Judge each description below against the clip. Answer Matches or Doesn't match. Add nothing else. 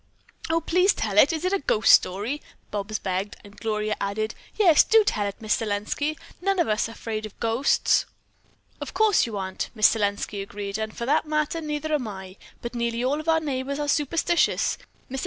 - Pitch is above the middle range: Matches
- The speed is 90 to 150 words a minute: Doesn't match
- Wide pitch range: Matches